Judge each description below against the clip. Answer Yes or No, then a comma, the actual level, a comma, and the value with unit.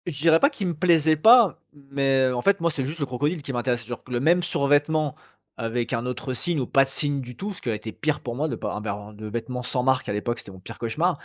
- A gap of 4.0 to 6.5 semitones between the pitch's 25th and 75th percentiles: Yes, average, 4.5 semitones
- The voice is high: No, low, 135 Hz